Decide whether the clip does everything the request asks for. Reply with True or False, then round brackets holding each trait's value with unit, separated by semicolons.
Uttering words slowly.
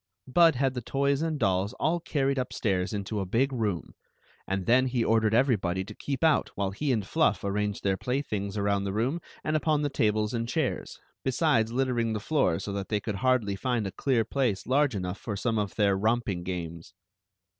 False (200 wpm)